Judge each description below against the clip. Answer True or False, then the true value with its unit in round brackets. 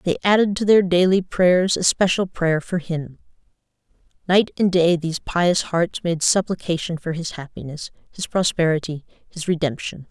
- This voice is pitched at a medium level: True (175 Hz)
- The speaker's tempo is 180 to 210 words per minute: False (155 wpm)